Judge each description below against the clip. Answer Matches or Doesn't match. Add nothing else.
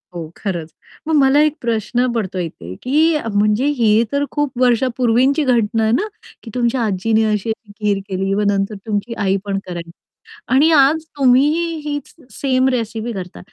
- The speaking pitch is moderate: Doesn't match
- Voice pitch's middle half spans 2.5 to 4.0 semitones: Doesn't match